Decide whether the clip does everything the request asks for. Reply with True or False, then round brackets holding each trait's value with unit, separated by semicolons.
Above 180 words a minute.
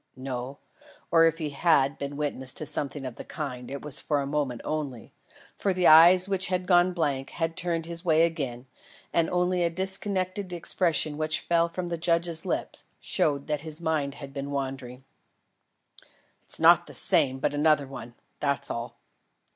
False (175 wpm)